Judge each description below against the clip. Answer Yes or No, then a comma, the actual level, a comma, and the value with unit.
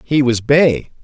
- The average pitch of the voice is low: Yes, low, 130 Hz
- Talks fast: No, average, 175 wpm